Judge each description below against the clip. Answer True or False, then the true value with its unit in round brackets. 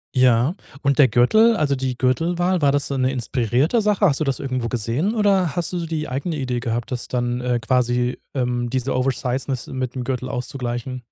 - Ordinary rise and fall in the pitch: True (3.4 semitones)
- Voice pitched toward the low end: True (130 Hz)